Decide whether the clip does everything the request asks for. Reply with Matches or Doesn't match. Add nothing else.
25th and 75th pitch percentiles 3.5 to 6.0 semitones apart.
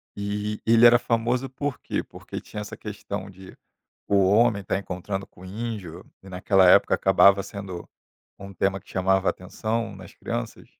Doesn't match